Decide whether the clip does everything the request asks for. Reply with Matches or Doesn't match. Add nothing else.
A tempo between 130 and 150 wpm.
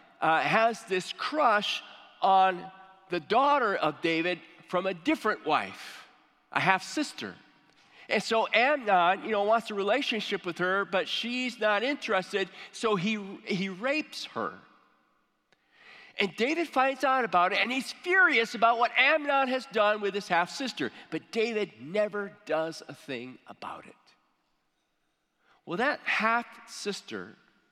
Matches